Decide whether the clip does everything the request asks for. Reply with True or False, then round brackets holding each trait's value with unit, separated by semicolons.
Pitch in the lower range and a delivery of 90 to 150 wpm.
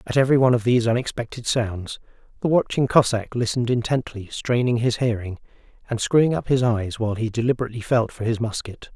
False (115 Hz; 180 wpm)